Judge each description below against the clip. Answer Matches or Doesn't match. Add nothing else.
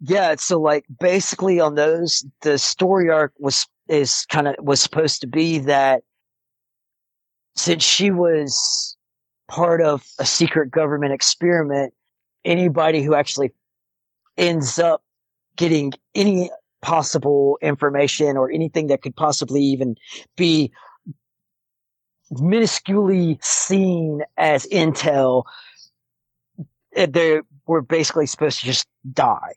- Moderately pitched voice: Matches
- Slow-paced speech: Matches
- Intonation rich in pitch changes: Doesn't match